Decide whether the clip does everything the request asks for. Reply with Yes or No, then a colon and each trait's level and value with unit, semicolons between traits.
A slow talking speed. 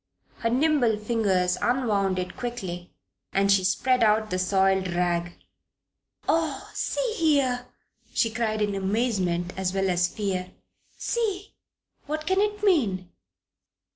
Yes: slow, 125 wpm